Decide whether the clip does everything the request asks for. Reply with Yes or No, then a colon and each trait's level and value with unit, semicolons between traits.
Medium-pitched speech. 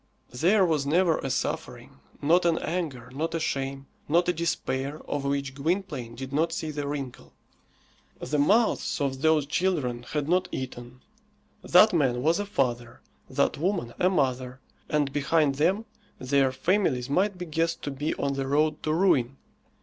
Yes: medium, 145 Hz